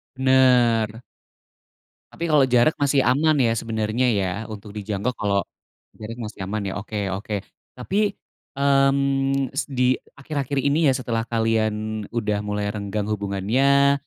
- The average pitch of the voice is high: No, low, 120 Hz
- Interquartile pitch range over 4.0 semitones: Yes, average, 4.4 semitones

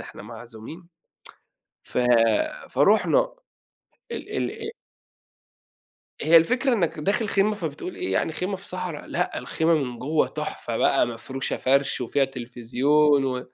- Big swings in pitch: Yes, wide, 6.1 semitones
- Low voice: No, medium, 150 Hz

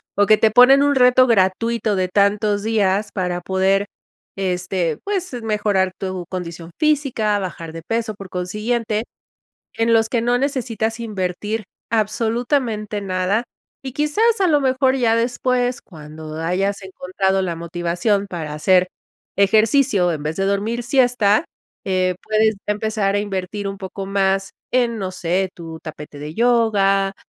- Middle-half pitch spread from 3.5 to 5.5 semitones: Yes, average, 3.8 semitones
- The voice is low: No, high, 205 Hz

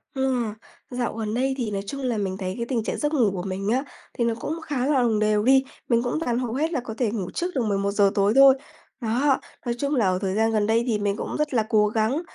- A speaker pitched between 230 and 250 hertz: Yes, high, 235 Hz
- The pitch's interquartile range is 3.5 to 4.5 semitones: Yes, average, 4.0 semitones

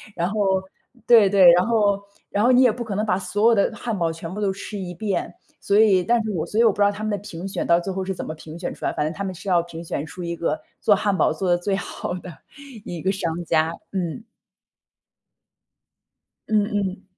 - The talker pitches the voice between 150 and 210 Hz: Yes, high, 195 Hz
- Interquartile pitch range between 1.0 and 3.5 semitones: Yes, average, 3.1 semitones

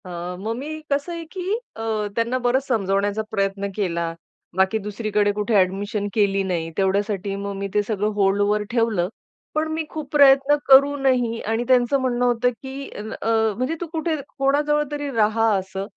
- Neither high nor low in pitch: No, high, 225 Hz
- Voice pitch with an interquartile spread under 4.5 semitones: No, average, 5.1 semitones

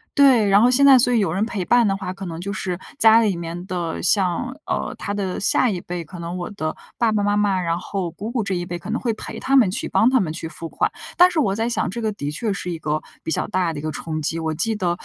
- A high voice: Yes, high, 195 Hz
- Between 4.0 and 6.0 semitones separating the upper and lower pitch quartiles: Yes, average, 4.5 semitones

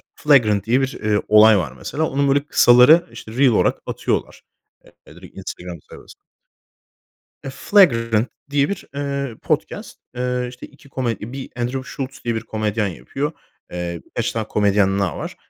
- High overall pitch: No, low, 120 Hz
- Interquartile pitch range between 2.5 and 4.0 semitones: No, average, 4.4 semitones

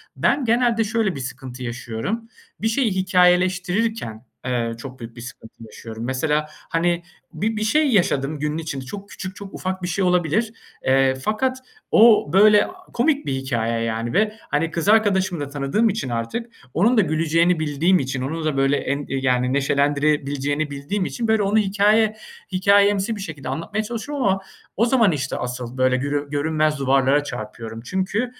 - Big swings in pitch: Yes, wide, 7.4 semitones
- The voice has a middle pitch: Yes, medium, 165 Hz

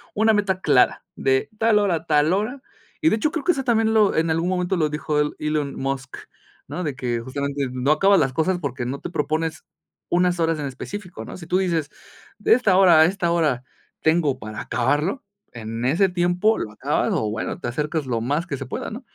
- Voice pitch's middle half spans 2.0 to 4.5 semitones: No, wide, 5.4 semitones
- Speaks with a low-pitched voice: No, medium, 160 Hz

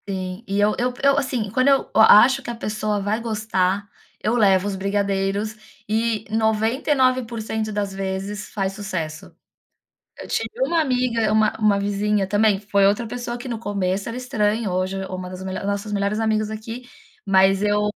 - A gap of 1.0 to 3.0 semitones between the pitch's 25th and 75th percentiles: Yes, narrow, 2.5 semitones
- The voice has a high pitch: Yes, high, 210 Hz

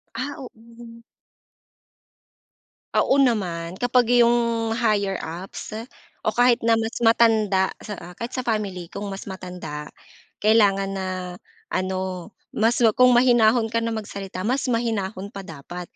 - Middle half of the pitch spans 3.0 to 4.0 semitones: Yes, average, 3.6 semitones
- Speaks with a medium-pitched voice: No, high, 220 Hz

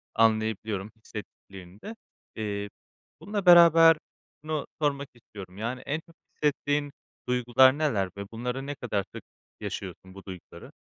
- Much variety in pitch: Yes, wide, 6.2 semitones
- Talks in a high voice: No, low, 120 Hz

